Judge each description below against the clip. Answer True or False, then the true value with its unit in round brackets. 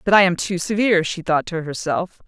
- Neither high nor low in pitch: True (175 Hz)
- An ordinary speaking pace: False (235 wpm)